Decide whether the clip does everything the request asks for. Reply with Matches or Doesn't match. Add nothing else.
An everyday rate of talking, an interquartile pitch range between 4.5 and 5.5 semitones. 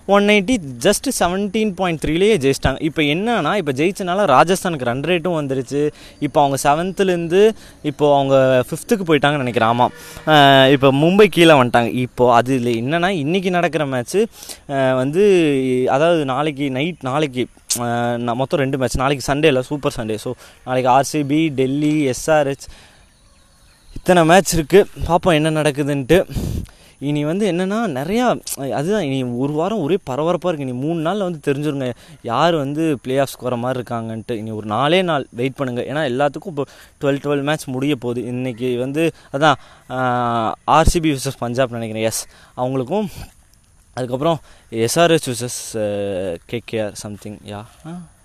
Doesn't match